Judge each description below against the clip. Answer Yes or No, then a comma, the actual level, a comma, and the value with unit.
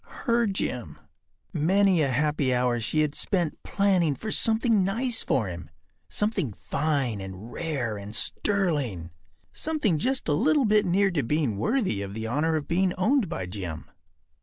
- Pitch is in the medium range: Yes, medium, 155 Hz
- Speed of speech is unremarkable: Yes, average, 155 wpm